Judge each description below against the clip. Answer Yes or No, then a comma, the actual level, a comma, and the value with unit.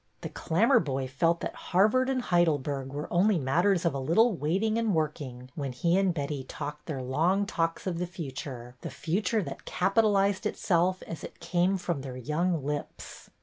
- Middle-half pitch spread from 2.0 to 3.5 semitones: No, average, 5.3 semitones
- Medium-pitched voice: Yes, medium, 170 Hz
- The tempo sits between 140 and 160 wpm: No, average, 180 wpm